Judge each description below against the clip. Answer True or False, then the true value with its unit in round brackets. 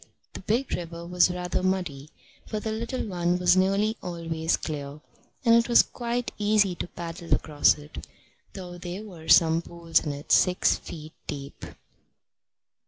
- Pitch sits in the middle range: True (175 Hz)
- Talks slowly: False (155 wpm)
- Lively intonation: False (3.8 semitones)